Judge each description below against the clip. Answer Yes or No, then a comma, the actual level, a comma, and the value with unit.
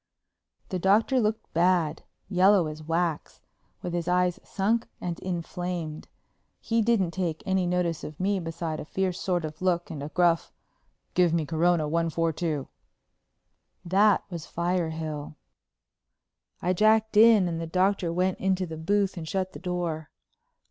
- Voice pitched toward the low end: No, medium, 175 Hz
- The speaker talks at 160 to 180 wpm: No, average, 150 wpm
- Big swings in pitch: No, narrow, 2.5 semitones